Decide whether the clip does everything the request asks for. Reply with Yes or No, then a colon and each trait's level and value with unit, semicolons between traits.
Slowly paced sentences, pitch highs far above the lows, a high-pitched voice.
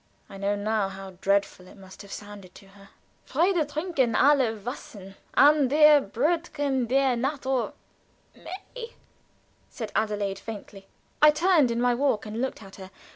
No: average, 155 wpm; wide, 6.3 semitones; high, 235 Hz